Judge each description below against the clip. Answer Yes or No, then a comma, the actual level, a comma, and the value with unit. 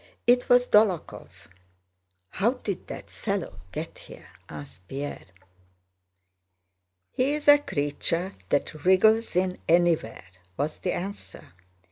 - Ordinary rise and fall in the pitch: No, wide, 7.5 semitones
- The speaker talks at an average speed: No, slow, 105 wpm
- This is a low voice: No, medium, 180 Hz